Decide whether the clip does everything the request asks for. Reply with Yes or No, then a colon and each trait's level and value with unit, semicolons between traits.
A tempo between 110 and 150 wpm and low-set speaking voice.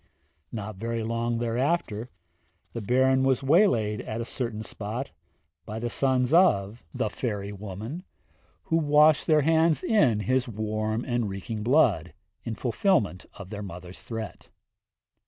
Yes: slow, 135 wpm; low, 115 Hz